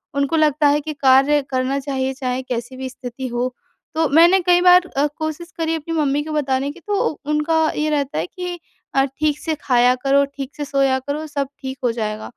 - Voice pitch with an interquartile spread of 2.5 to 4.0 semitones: Yes, average, 3.0 semitones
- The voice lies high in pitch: Yes, very high, 280 Hz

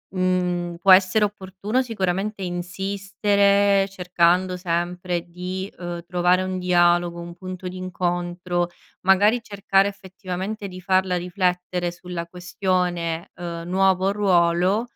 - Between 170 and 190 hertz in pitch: Yes, medium, 185 Hz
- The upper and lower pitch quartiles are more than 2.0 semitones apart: No, narrow, 1.7 semitones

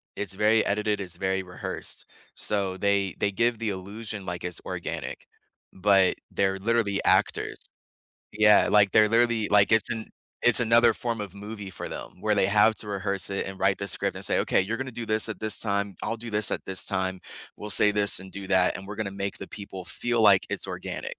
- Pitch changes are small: Yes, narrow, 2.1 semitones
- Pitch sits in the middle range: No, low, 100 Hz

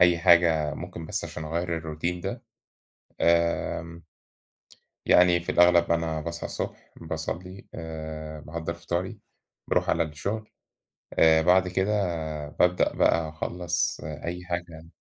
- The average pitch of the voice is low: Yes, very low, 85 Hz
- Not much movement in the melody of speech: Yes, narrow, 1.6 semitones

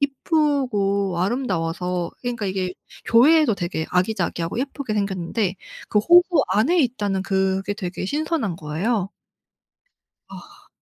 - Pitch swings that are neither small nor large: No, wide, 6.0 semitones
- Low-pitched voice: No, high, 205 Hz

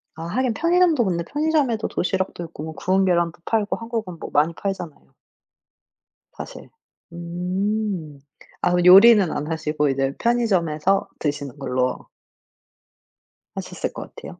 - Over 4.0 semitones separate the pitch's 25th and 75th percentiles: Yes, wide, 5.6 semitones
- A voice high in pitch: No, medium, 180 Hz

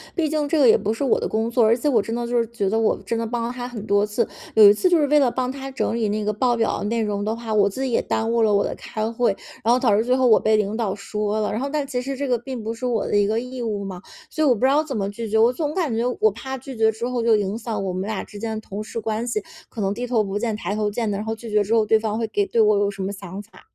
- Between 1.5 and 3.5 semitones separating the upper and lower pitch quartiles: Yes, average, 2.8 semitones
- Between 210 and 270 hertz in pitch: Yes, high, 225 Hz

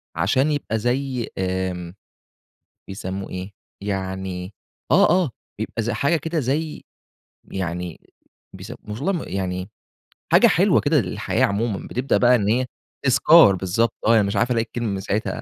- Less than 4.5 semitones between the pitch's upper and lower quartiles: No, average, 4.9 semitones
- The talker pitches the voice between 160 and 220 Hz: No, low, 105 Hz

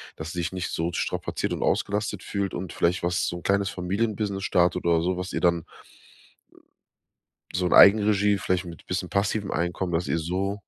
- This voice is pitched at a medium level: No, very low, 90 Hz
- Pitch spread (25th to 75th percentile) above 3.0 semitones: No, narrow, 2.2 semitones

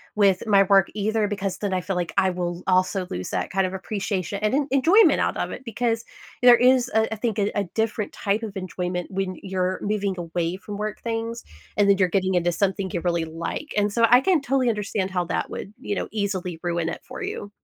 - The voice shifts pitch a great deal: No, average, 3.2 semitones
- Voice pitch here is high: Yes, high, 200 Hz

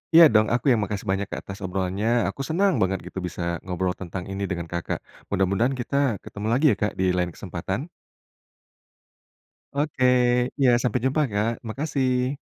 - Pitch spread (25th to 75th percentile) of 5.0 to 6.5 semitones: Yes, wide, 5.5 semitones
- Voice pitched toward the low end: Yes, low, 105 Hz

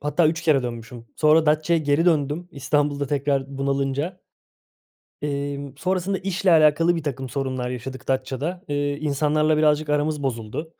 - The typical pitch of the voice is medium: Yes, medium, 145 Hz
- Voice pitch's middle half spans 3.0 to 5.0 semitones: No, narrow, 2.4 semitones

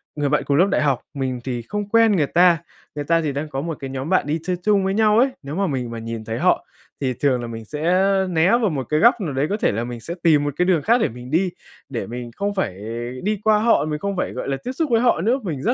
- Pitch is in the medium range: Yes, medium, 155 Hz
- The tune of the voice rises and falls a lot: Yes, wide, 7.0 semitones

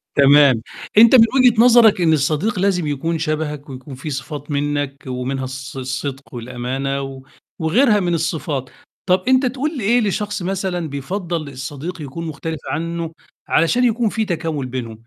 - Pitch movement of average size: No, wide, 6.1 semitones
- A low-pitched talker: No, medium, 155 Hz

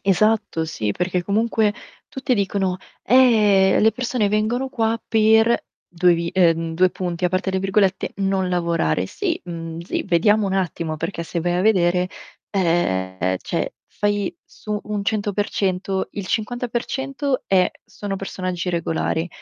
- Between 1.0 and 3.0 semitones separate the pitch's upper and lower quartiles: No, average, 3.5 semitones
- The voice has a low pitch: No, high, 190 Hz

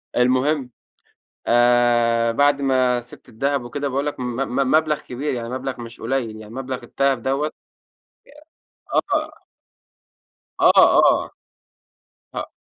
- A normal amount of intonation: No, narrow, 2.3 semitones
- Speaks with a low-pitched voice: Yes, low, 130 Hz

